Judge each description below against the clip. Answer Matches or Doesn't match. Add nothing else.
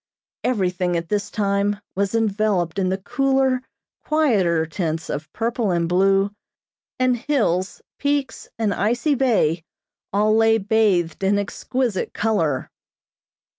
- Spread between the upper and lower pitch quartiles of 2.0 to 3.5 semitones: Doesn't match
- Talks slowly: Matches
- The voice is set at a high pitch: Matches